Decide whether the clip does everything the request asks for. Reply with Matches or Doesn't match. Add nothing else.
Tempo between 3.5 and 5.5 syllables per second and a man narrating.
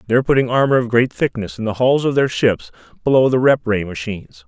Doesn't match